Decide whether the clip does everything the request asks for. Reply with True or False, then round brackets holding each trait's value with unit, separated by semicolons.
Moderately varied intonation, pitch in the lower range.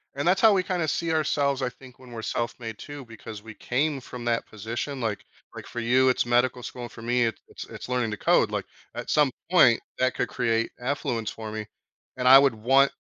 True (3.2 semitones; 125 Hz)